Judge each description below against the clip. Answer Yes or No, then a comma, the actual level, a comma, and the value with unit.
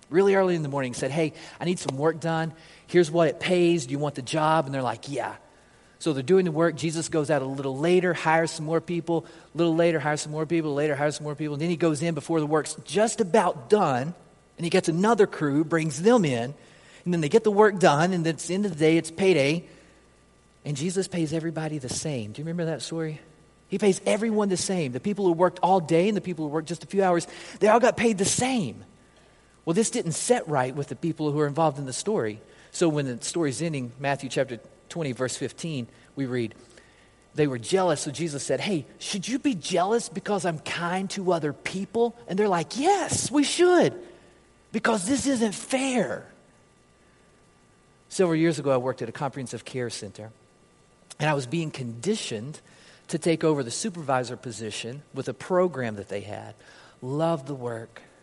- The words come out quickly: Yes, fast, 215 wpm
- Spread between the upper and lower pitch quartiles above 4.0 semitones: Yes, average, 4.4 semitones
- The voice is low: No, medium, 165 Hz